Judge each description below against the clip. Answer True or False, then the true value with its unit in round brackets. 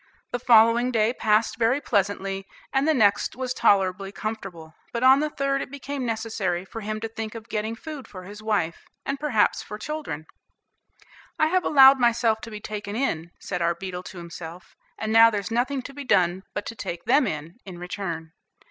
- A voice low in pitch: False (220 Hz)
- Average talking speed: True (195 wpm)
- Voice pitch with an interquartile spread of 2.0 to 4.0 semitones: False (4.6 semitones)